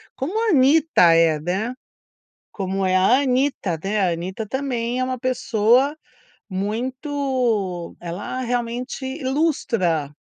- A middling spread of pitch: No, wide, 5.7 semitones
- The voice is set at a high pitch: Yes, high, 235 Hz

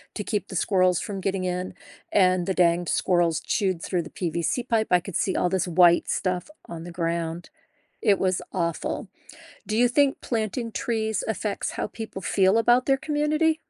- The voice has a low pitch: No, high, 190 Hz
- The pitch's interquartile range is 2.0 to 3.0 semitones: No, average, 4.1 semitones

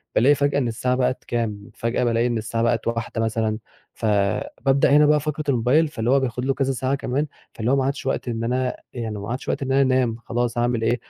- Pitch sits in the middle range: No, low, 125 Hz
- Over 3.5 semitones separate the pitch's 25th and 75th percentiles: No, average, 2.8 semitones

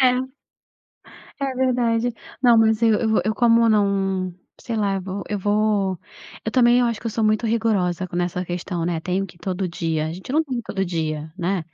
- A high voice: Yes, high, 205 Hz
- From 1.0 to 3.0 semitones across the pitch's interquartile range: No, average, 4.2 semitones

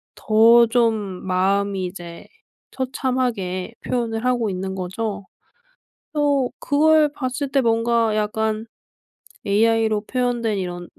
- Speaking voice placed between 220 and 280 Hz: Yes, high, 225 Hz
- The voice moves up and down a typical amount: Yes, average, 3.9 semitones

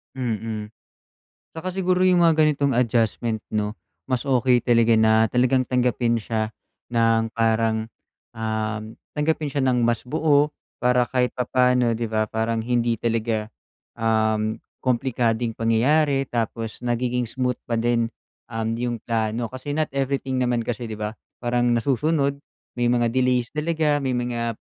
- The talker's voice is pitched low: Yes, low, 120 Hz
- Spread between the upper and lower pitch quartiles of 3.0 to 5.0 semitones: No, narrow, 2.4 semitones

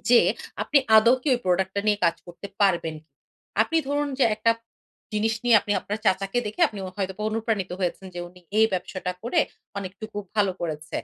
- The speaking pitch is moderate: No, high, 205 Hz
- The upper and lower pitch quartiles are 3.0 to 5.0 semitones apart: Yes, average, 3.3 semitones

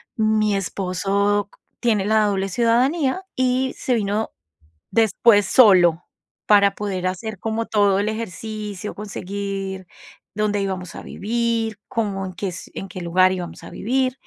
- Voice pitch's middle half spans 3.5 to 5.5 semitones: No, average, 2.7 semitones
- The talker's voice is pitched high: Yes, high, 205 Hz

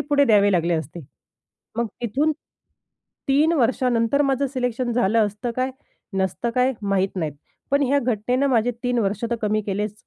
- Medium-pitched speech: No, high, 235 Hz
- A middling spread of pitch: Yes, average, 4.4 semitones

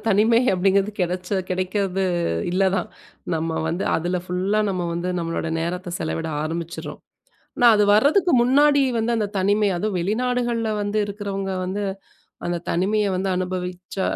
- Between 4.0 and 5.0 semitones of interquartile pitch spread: No, average, 2.9 semitones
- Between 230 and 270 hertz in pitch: No, high, 195 Hz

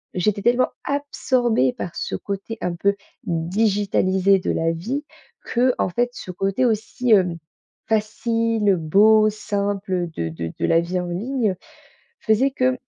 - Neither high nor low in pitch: No, high, 205 Hz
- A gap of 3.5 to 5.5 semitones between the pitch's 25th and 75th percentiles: Yes, average, 4.1 semitones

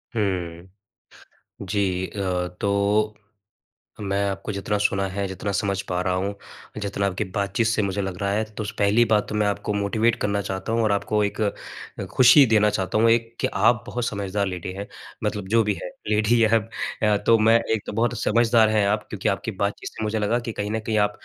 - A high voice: No, low, 105 Hz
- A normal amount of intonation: No, narrow, 2.0 semitones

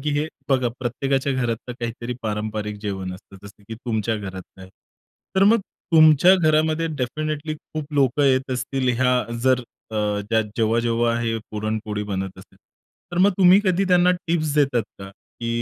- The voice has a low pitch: Yes, low, 125 Hz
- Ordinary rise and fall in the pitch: No, wide, 6.0 semitones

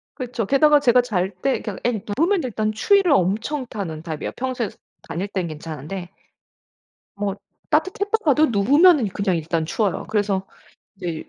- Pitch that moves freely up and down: Yes, wide, 7.5 semitones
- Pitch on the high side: Yes, high, 215 Hz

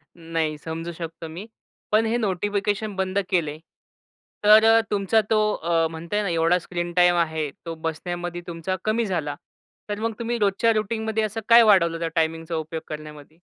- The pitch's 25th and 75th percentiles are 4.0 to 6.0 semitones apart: Yes, average, 4.5 semitones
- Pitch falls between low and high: Yes, medium, 175 Hz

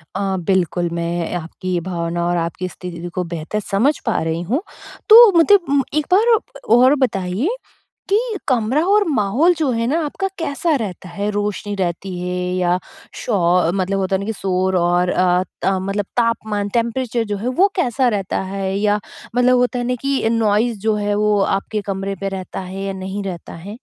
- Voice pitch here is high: Yes, high, 200 Hz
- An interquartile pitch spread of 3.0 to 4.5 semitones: No, average, 4.9 semitones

